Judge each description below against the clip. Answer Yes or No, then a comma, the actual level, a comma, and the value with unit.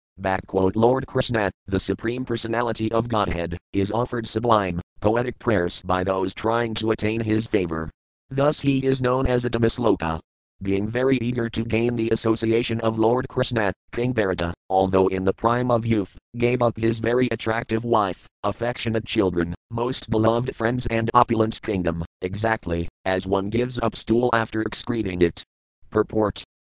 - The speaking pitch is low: Yes, low, 110 Hz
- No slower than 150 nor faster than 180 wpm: Yes, average, 160 wpm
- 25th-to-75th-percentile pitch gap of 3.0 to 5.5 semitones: Yes, average, 3.8 semitones